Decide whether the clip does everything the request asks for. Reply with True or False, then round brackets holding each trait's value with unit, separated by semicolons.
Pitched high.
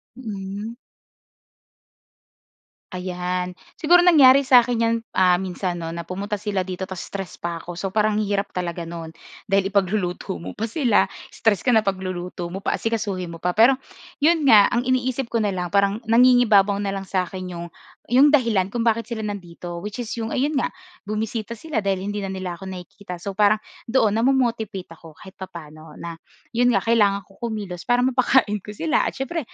True (200 Hz)